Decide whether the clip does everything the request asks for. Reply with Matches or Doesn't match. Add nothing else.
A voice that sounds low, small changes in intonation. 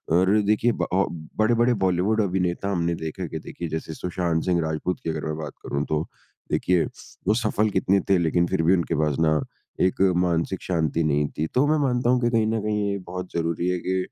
Doesn't match